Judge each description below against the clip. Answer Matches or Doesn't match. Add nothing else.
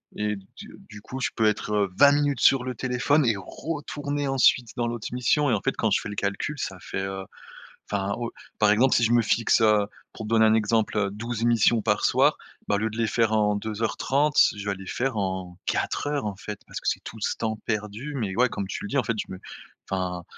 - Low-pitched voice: Matches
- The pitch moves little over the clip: Doesn't match